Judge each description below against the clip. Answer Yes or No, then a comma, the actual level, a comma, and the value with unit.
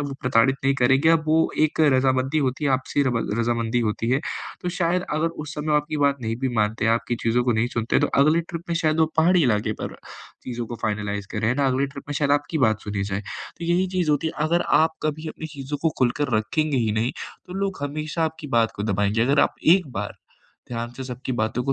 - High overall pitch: No, low, 135 Hz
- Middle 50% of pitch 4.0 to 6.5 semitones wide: Yes, average, 5.0 semitones